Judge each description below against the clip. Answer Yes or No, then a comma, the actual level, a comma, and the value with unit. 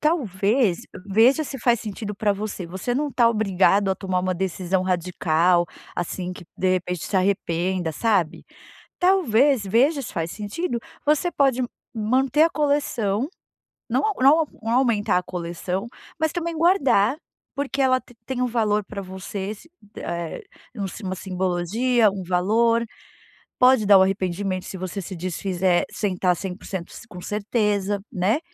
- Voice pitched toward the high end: Yes, high, 205 Hz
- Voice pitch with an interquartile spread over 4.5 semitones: Yes, average, 5.1 semitones